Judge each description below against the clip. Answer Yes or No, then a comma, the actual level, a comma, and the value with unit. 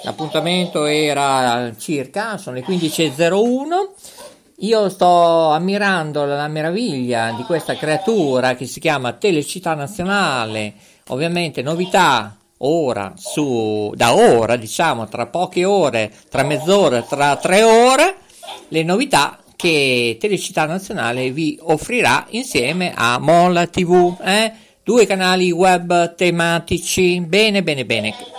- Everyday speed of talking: No, slow, 110 wpm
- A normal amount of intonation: Yes, average, 4.9 semitones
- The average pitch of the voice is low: No, medium, 165 Hz